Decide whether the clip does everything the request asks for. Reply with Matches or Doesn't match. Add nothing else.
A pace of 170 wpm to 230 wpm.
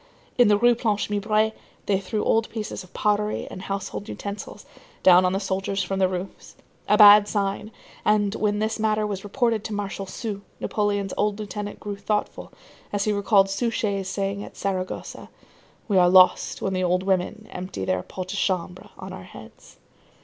Matches